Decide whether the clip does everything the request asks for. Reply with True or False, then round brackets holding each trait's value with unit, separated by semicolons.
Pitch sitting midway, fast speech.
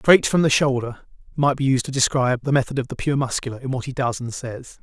False (130 Hz; 260 wpm)